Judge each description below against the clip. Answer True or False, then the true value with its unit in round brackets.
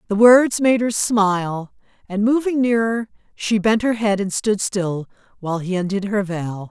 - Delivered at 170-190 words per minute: True (180 wpm)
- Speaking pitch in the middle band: False (210 Hz)